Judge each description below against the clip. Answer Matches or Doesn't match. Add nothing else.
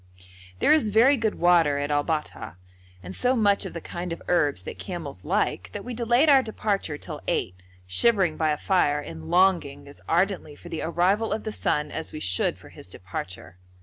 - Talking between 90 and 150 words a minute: Doesn't match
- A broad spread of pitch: Matches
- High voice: Doesn't match